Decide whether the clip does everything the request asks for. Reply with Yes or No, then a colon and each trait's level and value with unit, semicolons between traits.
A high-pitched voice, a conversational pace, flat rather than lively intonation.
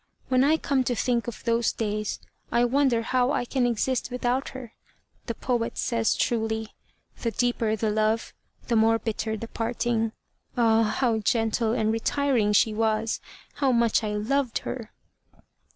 Yes: high, 230 Hz; average, 155 wpm; narrow, 2.0 semitones